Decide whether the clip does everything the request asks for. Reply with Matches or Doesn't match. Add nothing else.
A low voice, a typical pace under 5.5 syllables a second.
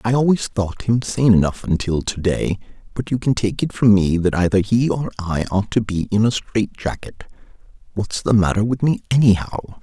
Matches